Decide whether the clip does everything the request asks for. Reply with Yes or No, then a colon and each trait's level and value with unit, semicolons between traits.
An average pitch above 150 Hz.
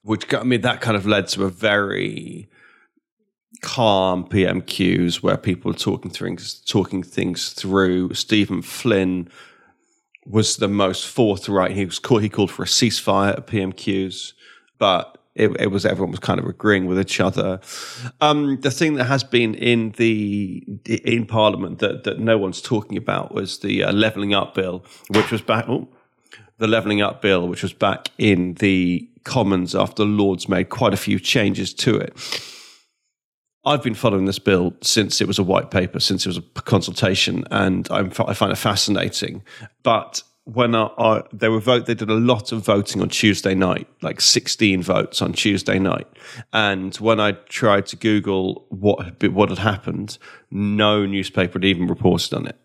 No: low, 105 Hz